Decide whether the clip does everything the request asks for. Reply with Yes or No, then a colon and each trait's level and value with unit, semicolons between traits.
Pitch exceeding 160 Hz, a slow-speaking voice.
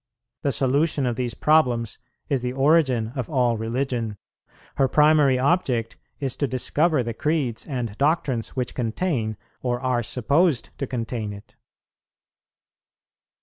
No: low, 130 Hz; slow, 130 wpm